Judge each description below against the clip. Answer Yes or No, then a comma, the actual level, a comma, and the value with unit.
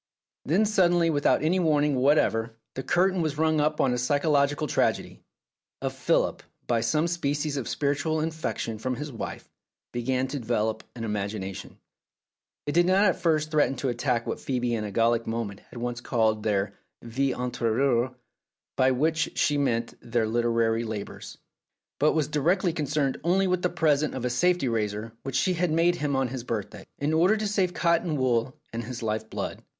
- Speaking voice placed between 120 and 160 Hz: Yes, low, 135 Hz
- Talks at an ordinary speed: Yes, average, 180 wpm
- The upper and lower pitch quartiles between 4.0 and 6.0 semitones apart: Yes, average, 5.2 semitones